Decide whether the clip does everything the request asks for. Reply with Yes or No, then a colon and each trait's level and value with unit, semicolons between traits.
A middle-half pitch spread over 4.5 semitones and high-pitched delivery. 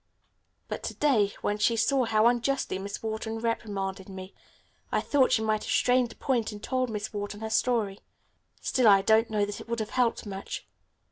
No: average, 2.7 semitones; high, 220 Hz